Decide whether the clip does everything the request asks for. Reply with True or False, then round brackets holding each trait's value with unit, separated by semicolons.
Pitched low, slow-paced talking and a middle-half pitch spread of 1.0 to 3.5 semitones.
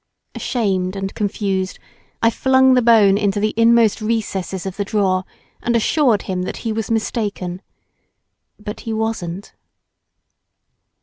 False (210 Hz; 130 wpm; 2.9 semitones)